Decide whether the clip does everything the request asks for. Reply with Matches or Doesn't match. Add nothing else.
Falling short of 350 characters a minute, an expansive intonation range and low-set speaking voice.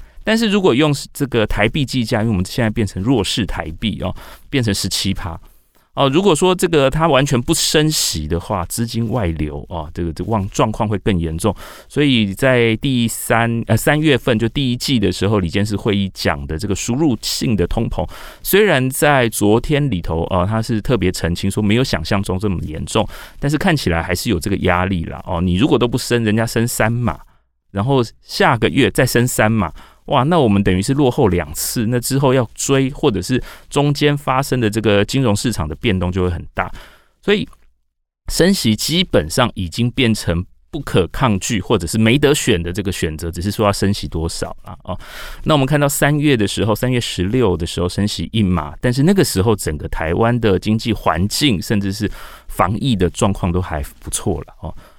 Matches